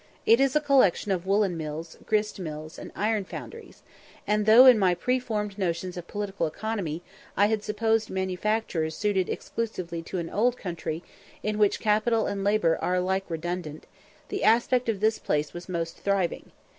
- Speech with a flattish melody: No, average, 3.9 semitones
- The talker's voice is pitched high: Yes, high, 200 Hz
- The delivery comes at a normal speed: Yes, average, 170 wpm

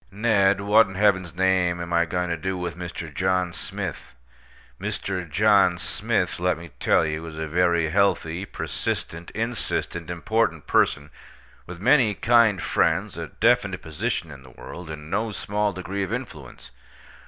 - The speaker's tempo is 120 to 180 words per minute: Yes, average, 155 wpm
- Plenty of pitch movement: No, average, 3.2 semitones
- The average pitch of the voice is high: No, very low, 90 Hz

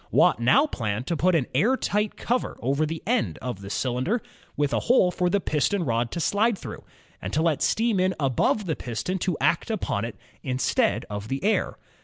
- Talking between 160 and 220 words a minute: Yes, fast, 205 wpm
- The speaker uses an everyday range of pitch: No, wide, 8.1 semitones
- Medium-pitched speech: Yes, medium, 160 Hz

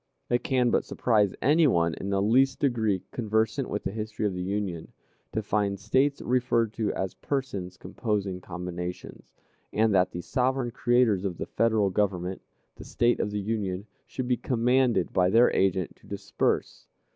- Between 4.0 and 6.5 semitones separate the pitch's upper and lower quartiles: Yes, average, 4.3 semitones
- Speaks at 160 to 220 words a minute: Yes, average, 170 wpm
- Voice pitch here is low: Yes, low, 105 Hz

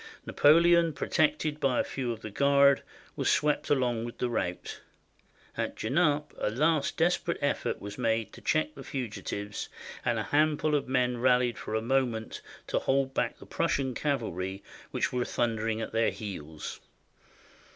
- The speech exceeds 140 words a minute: Yes, average, 165 wpm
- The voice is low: Yes, low, 130 Hz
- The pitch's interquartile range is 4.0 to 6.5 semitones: Yes, average, 4.7 semitones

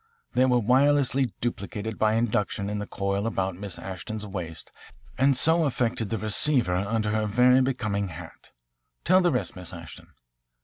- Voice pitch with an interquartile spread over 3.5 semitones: Yes, average, 4.3 semitones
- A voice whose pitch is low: Yes, low, 110 Hz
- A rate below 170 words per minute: Yes, average, 160 wpm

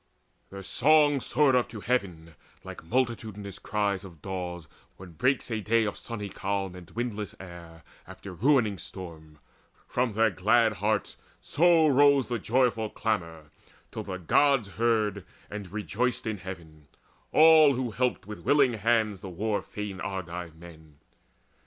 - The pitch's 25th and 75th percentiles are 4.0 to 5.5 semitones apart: Yes, average, 4.7 semitones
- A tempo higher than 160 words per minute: No, average, 150 wpm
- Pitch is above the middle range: No, low, 105 Hz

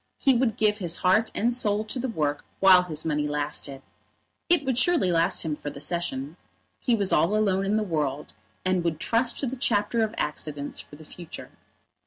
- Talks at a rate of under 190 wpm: No, average, 200 wpm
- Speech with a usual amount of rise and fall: No, wide, 6.5 semitones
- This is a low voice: No, medium, 185 Hz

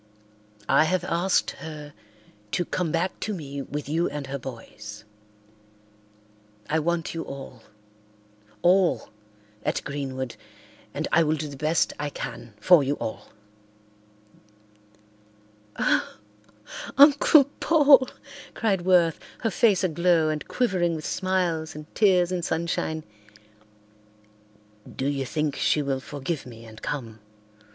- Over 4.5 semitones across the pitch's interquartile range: Yes, average, 4.9 semitones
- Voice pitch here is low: No, medium, 155 Hz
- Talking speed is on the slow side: Yes, slow, 120 wpm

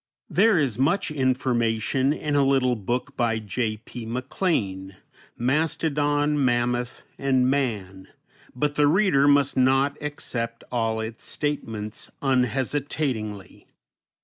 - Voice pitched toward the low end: Yes, low, 130 Hz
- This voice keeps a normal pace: No, slow, 110 wpm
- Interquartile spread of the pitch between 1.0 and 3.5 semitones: No, average, 4.0 semitones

